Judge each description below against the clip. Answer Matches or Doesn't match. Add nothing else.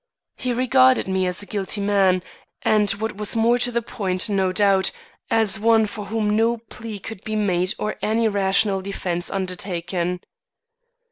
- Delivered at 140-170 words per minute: Matches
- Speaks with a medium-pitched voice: Doesn't match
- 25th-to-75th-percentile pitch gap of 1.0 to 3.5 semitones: Matches